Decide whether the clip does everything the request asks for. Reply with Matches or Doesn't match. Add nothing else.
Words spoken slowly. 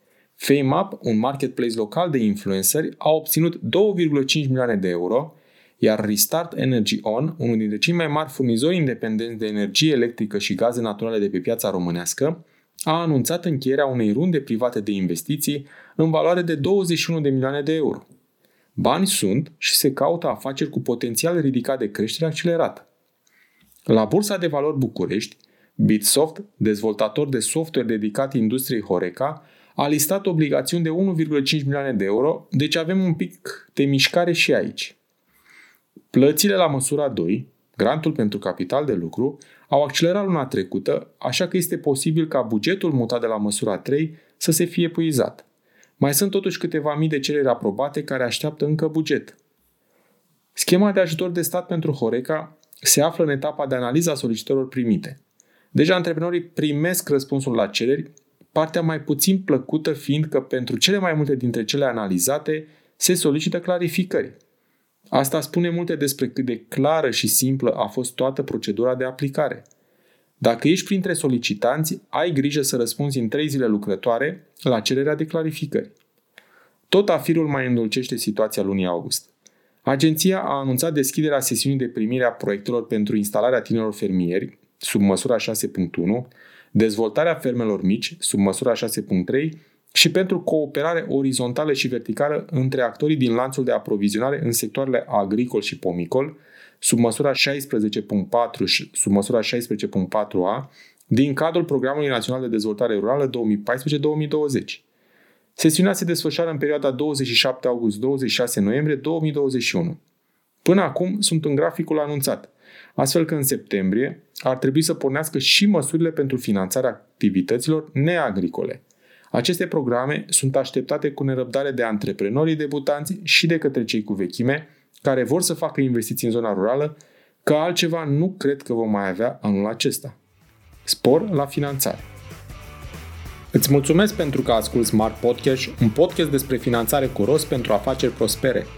Doesn't match